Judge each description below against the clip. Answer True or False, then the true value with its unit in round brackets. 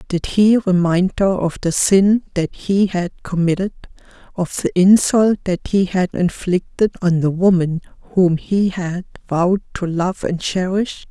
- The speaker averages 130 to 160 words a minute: True (150 wpm)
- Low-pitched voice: False (185 Hz)